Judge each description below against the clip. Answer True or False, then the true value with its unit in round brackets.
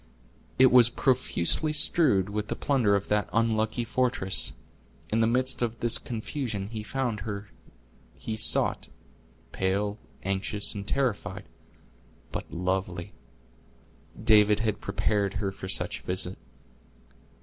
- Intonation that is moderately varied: True (3.2 semitones)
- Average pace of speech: False (125 wpm)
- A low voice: True (105 Hz)